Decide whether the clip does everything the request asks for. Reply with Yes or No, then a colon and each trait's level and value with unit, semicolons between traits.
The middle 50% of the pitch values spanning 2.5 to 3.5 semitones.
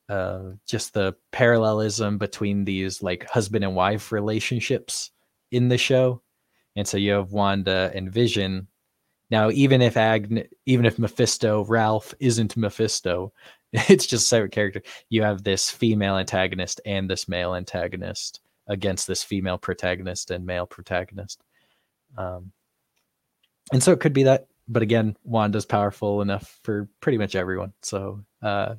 Yes: average, 2.9 semitones